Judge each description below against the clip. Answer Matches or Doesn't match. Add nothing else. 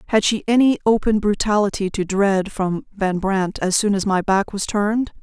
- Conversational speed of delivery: Matches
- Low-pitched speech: Doesn't match